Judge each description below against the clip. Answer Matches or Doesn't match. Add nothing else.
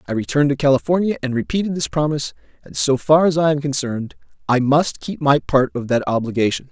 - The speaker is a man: Matches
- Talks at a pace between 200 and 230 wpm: Matches